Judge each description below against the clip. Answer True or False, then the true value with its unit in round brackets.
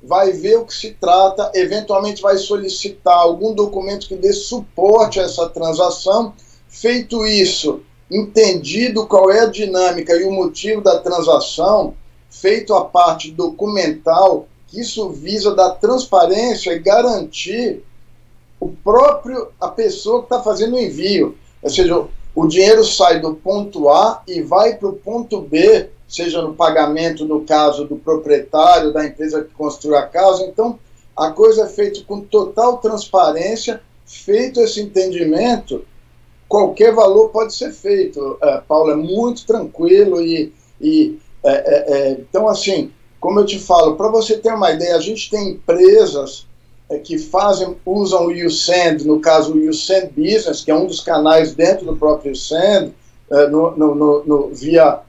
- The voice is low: False (195 Hz)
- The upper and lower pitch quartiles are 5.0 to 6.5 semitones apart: True (5.3 semitones)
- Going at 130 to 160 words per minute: True (155 wpm)